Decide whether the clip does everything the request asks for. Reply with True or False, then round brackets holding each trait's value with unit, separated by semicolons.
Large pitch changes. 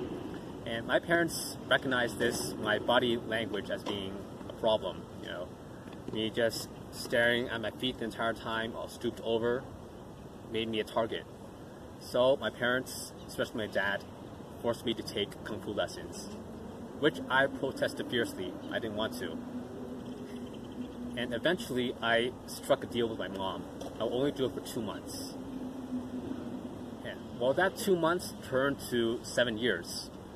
False (2.5 semitones)